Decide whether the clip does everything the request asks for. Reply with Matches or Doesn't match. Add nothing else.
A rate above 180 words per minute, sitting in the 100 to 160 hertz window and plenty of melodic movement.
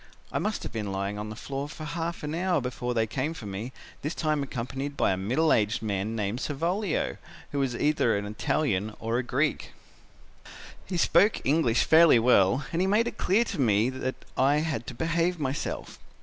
Matches